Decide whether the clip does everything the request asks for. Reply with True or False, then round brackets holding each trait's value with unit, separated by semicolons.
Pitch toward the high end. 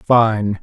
False (110 Hz)